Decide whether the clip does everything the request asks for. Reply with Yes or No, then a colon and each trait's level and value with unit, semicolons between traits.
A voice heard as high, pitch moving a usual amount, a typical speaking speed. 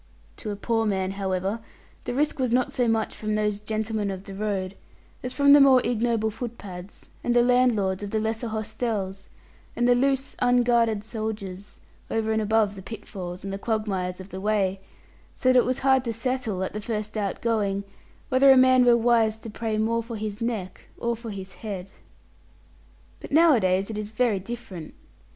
Yes: high, 220 Hz; average, 3.3 semitones; average, 185 wpm